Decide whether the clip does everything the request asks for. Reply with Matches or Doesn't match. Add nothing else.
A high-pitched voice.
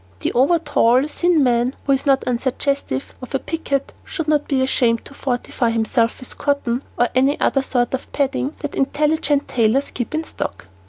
Matches